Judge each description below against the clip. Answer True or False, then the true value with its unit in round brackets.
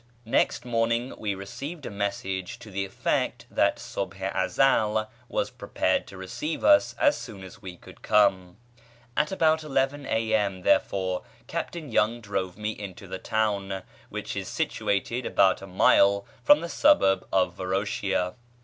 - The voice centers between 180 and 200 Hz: False (100 Hz)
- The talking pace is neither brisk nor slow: True (150 wpm)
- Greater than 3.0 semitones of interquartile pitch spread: True (3.8 semitones)